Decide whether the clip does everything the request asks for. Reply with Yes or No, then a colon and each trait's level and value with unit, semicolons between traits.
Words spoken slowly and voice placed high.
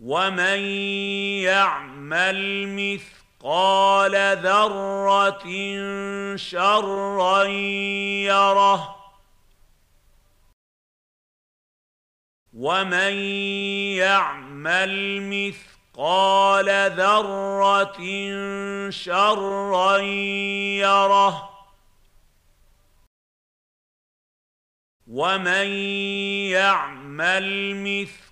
Yes: slow, 30 wpm; high, 195 Hz